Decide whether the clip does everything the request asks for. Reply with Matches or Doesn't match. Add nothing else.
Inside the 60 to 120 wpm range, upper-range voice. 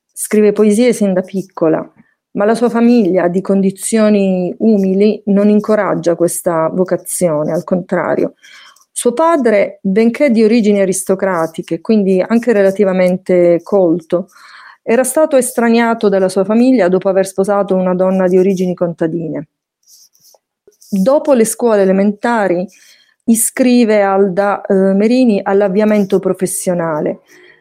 Matches